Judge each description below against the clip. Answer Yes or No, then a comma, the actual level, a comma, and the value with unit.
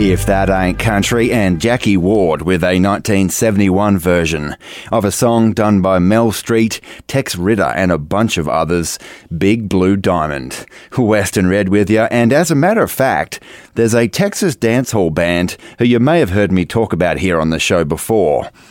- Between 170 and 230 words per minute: Yes, average, 185 wpm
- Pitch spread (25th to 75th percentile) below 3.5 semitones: No, average, 3.9 semitones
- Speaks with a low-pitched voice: Yes, low, 100 Hz